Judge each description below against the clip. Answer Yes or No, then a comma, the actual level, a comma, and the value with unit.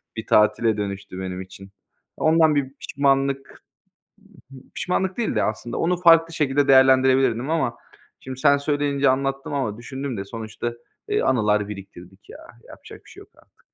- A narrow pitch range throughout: No, average, 5.0 semitones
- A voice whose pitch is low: Yes, low, 130 Hz